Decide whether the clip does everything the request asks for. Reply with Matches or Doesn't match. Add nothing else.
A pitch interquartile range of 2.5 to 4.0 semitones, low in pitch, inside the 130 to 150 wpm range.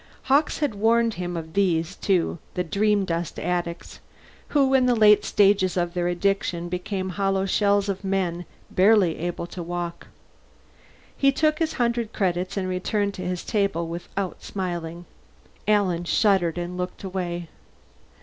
Doesn't match